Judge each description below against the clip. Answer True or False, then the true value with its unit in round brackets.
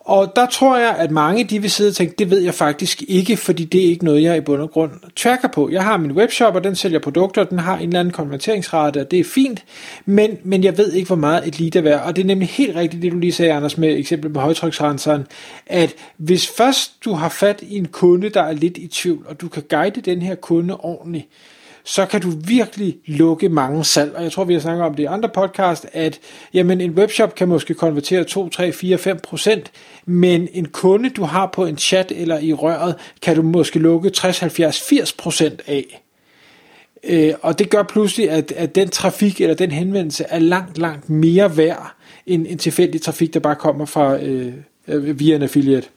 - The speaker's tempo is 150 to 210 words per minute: False (225 wpm)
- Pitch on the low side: False (175 Hz)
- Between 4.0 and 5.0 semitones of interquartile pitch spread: False (3.3 semitones)